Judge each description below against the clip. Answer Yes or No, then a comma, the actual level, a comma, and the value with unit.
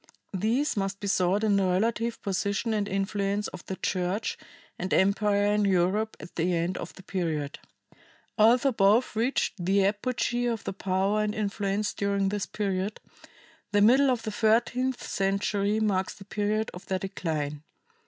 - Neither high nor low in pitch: No, high, 200 Hz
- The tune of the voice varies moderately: No, narrow, 2.3 semitones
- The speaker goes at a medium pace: Yes, average, 160 wpm